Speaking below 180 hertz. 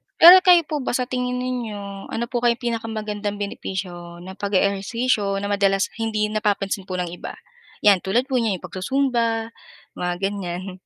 No: high, 205 Hz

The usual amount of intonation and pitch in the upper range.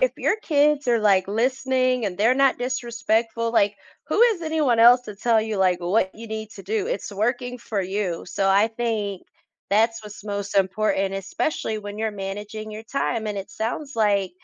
Yes: average, 3.2 semitones; high, 220 Hz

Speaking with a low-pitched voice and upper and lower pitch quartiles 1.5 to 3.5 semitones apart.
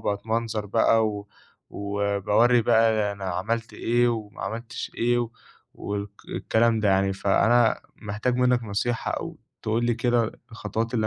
Yes: low, 110 Hz; narrow, 2.5 semitones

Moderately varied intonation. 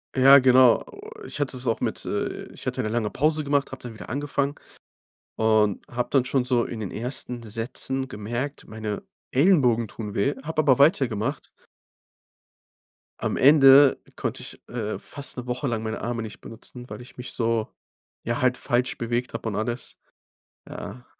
Yes: average, 3.2 semitones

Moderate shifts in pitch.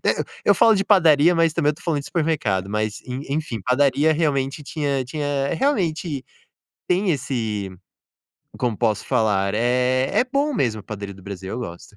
No: wide, 6.5 semitones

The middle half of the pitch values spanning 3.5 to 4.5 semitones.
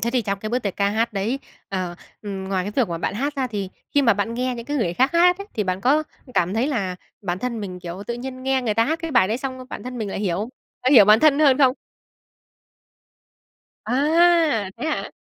No: average, 5.2 semitones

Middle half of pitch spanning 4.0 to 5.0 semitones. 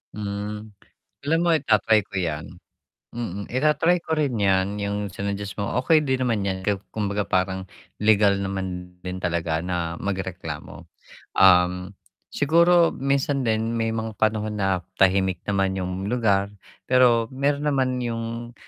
Yes: average, 4.3 semitones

